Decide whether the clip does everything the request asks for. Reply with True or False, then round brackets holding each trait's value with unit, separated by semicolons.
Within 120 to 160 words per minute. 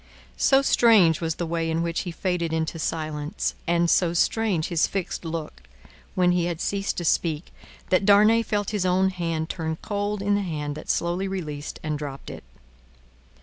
False (180 wpm)